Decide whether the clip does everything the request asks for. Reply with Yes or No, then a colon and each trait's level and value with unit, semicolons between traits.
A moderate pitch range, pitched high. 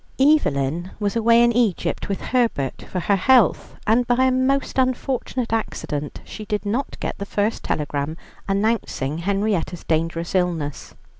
No: wide, 6.3 semitones; high, 205 Hz